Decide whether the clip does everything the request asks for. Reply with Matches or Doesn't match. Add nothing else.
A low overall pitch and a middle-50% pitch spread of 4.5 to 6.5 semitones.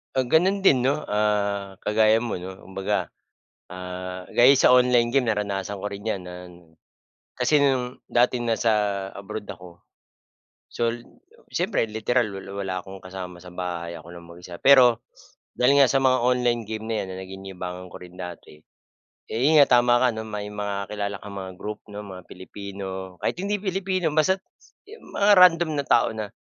Matches